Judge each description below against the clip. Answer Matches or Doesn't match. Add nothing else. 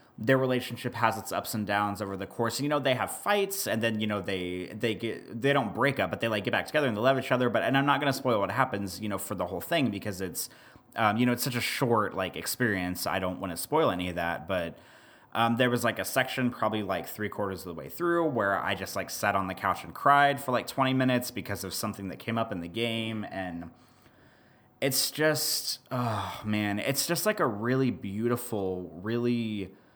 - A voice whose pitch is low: Matches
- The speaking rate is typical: Doesn't match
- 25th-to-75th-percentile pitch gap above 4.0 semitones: Matches